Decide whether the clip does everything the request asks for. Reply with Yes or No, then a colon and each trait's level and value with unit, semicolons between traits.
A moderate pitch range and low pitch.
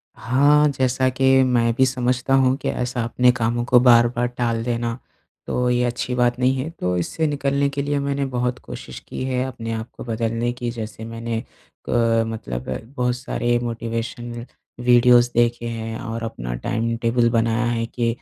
No: narrow, 1.7 semitones; low, 120 Hz